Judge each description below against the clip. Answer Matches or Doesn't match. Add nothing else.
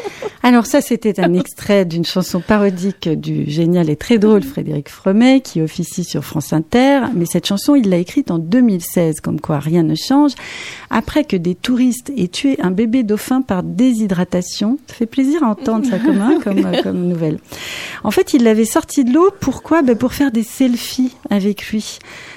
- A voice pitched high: Matches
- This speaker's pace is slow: Doesn't match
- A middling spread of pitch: Doesn't match